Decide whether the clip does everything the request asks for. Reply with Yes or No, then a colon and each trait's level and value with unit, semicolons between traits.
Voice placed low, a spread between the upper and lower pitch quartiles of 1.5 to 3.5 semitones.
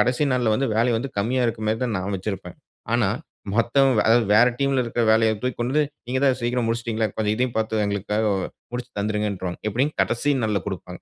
Yes: low, 115 Hz; average, 2.8 semitones